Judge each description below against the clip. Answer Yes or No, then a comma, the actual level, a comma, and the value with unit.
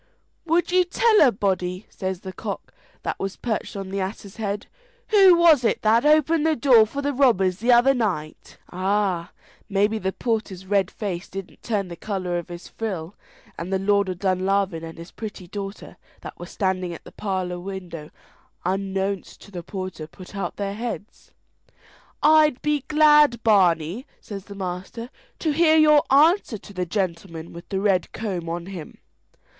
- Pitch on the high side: Yes, high, 195 Hz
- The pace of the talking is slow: No, average, 170 wpm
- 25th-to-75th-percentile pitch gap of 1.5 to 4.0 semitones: No, average, 4.5 semitones